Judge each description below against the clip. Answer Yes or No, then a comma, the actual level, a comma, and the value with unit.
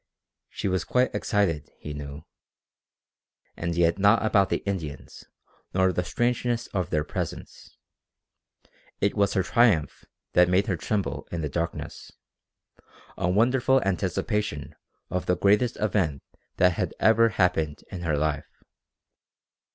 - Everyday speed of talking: No, slow, 130 wpm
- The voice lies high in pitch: No, very low, 95 Hz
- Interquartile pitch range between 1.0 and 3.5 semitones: No, average, 4.1 semitones